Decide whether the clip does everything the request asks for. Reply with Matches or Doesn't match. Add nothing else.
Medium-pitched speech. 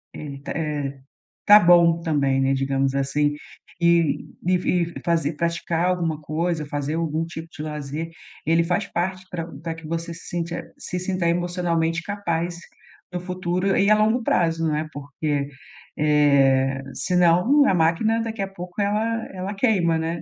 Matches